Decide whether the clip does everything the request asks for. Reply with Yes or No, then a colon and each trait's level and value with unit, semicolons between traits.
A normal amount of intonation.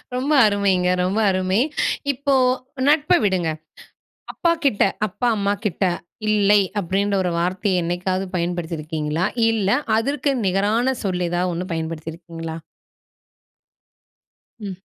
Yes: average, 3.3 semitones